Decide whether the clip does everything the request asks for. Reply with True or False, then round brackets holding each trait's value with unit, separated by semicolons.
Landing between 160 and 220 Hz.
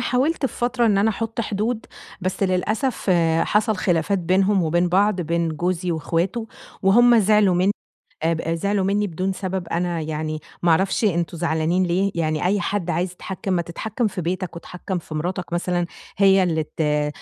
True (185 Hz)